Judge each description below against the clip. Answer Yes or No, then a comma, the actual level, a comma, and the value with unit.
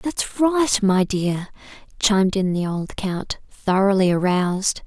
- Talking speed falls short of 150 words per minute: Yes, slow, 135 wpm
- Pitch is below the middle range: No, high, 200 Hz